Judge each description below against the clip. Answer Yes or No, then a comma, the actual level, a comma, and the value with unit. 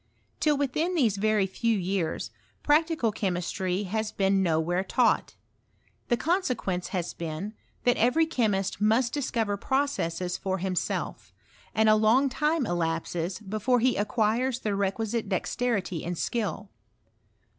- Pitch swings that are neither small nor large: Yes, average, 4.8 semitones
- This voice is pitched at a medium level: No, high, 215 Hz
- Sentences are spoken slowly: Yes, slow, 125 wpm